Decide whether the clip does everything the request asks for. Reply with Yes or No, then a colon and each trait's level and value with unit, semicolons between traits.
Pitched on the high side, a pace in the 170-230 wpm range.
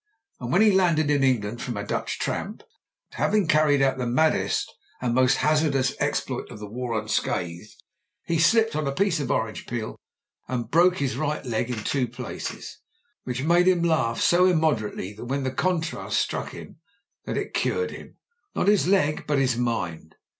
No: medium, 140 Hz; average, 185 wpm